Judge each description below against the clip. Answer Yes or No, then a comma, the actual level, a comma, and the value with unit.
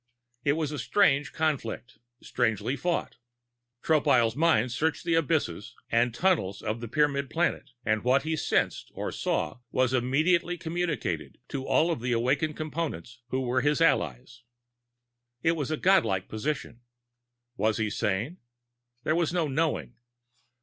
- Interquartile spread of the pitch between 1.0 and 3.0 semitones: No, wide, 5.4 semitones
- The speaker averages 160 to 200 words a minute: No, average, 145 wpm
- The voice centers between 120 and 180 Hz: Yes, medium, 140 Hz